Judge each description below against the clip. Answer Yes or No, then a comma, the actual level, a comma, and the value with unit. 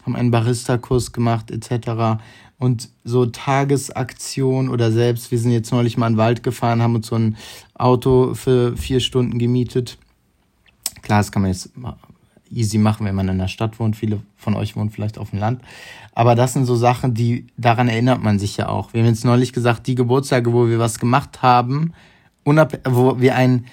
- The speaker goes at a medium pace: No, fast, 195 wpm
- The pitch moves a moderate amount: No, narrow, 2.0 semitones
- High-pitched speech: No, low, 120 Hz